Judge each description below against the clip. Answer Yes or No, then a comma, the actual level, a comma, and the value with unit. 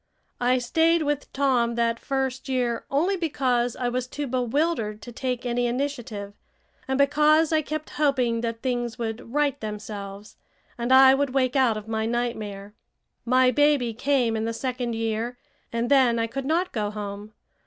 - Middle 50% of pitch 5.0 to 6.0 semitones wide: No, average, 3.2 semitones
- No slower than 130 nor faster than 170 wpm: Yes, average, 165 wpm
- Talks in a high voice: Yes, high, 245 Hz